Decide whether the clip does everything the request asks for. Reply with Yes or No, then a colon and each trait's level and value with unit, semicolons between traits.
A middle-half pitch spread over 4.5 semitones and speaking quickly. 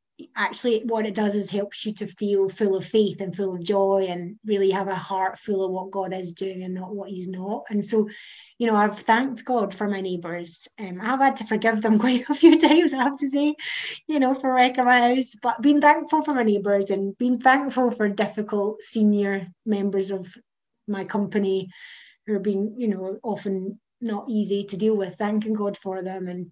No: average, 3.2 semitones; fast, 215 wpm